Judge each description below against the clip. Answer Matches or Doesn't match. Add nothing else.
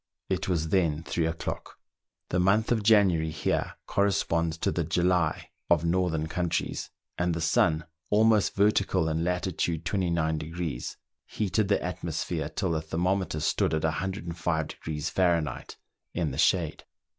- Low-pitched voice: Matches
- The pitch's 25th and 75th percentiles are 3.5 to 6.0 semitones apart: Doesn't match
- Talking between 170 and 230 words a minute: Doesn't match